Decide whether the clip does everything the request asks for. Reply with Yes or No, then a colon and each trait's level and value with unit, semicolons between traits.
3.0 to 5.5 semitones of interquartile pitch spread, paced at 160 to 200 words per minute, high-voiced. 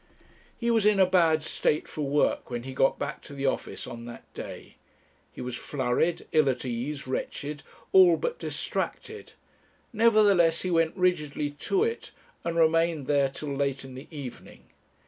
No: average, 4.7 semitones; average, 165 wpm; medium, 150 Hz